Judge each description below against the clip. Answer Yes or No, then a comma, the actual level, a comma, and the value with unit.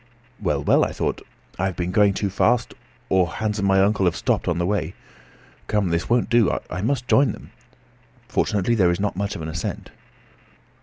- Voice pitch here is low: Yes, low, 100 Hz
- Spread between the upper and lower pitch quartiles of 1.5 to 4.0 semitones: Yes, average, 3.0 semitones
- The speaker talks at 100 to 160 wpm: No, average, 200 wpm